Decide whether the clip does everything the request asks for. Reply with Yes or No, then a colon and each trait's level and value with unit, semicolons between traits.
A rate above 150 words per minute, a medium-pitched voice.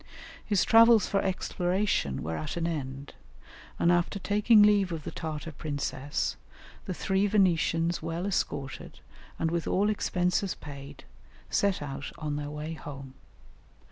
No: average, 140 wpm; medium, 170 Hz